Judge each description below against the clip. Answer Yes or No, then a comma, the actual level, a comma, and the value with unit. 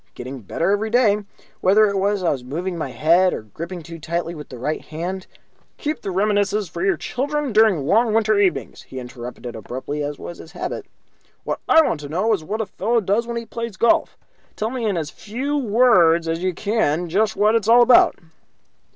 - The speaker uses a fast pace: Yes, fast, 215 wpm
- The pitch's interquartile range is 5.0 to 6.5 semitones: Yes, wide, 5.5 semitones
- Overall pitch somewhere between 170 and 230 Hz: Yes, high, 190 Hz